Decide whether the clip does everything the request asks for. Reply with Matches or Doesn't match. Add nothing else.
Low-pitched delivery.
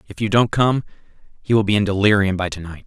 Matches